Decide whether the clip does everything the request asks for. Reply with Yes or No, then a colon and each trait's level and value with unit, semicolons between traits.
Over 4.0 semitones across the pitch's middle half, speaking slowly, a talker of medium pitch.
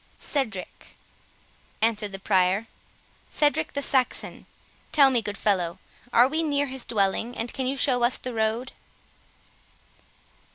No: average, 4.5 semitones; slow, 125 wpm; high, 235 Hz